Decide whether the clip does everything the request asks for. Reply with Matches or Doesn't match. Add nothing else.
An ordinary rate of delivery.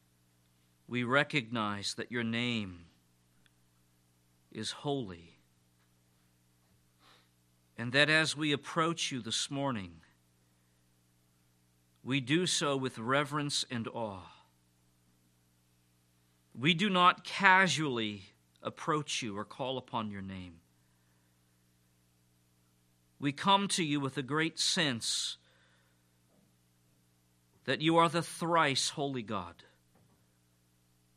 Doesn't match